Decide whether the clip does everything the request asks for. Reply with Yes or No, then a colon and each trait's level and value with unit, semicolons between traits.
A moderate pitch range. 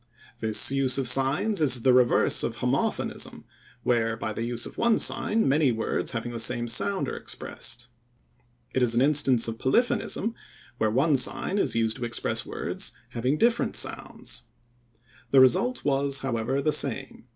Yes: average, 3.2 semitones